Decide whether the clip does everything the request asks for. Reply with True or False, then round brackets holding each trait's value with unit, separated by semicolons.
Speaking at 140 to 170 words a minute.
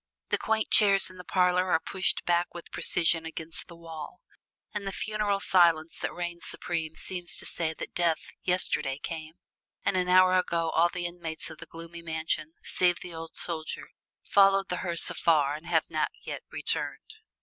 False (180 wpm)